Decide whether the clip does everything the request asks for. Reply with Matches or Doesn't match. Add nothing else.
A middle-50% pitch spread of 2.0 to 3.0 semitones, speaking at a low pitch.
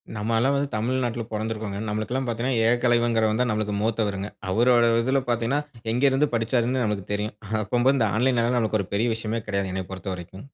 Matches